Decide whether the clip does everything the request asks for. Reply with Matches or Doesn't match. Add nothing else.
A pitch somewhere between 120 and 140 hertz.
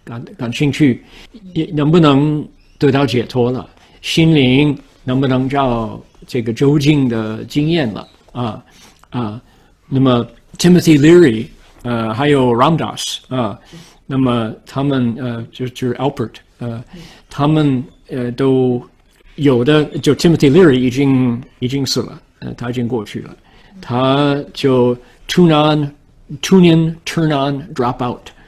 Matches